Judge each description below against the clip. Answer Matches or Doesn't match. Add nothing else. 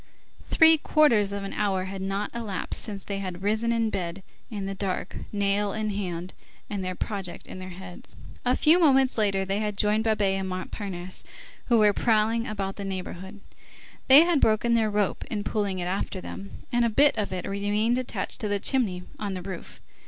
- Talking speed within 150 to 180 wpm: Doesn't match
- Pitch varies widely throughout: Doesn't match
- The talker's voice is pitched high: Matches